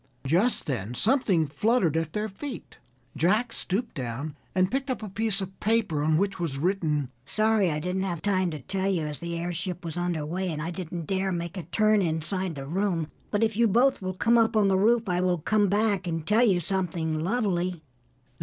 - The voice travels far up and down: No, average, 4.4 semitones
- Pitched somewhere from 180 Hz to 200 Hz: Yes, medium, 185 Hz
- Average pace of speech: No, fast, 210 wpm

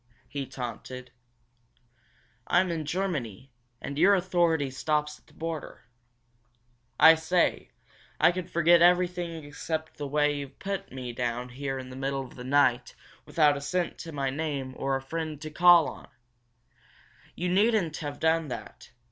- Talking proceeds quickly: No, average, 155 wpm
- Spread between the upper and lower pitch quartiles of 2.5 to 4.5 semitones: Yes, average, 4.0 semitones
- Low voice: No, medium, 150 Hz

